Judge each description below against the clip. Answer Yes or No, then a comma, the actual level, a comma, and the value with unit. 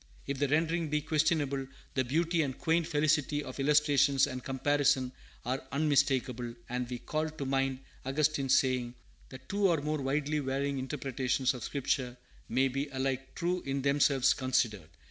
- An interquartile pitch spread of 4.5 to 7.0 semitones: No, narrow, 2.4 semitones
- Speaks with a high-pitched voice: No, medium, 140 Hz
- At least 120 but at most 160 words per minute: Yes, average, 155 wpm